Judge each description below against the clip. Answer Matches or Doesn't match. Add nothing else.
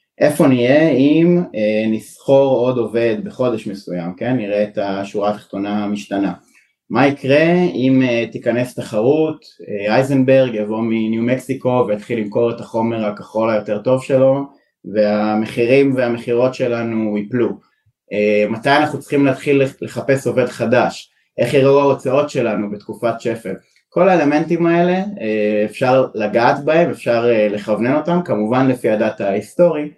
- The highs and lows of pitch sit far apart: Doesn't match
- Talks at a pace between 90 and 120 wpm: Doesn't match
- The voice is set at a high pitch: Doesn't match